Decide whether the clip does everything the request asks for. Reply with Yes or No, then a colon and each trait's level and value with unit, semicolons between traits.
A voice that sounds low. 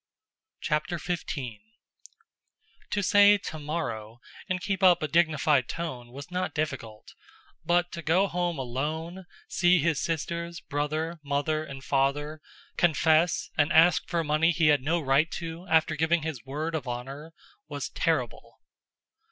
No: medium, 160 Hz